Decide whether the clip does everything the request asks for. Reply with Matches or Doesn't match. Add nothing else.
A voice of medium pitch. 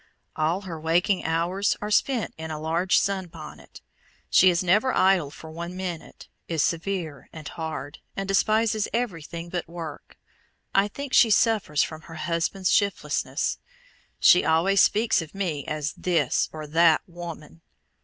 Matches